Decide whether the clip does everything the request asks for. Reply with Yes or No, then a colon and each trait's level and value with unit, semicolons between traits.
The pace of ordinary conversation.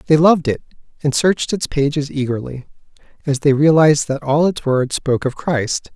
Yes: average, 180 wpm